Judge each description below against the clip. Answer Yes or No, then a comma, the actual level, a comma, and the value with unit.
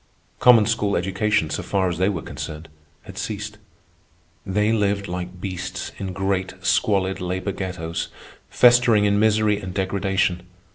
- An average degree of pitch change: No, narrow, 2.2 semitones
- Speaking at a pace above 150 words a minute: No, average, 140 wpm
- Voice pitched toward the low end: Yes, very low, 95 Hz